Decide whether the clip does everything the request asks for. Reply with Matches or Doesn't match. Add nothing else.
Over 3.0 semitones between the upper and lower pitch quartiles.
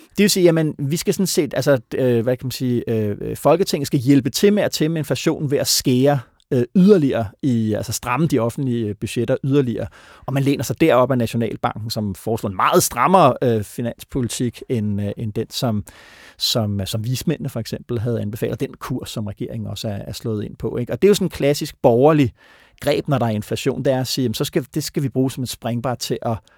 Matches